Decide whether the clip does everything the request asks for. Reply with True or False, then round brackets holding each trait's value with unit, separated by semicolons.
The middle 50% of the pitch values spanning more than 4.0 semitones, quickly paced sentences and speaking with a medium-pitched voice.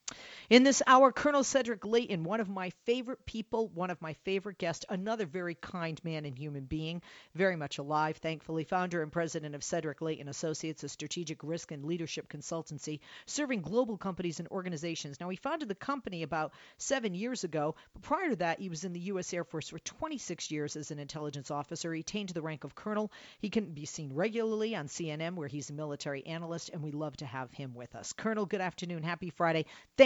True (5.1 semitones; 210 wpm; 170 Hz)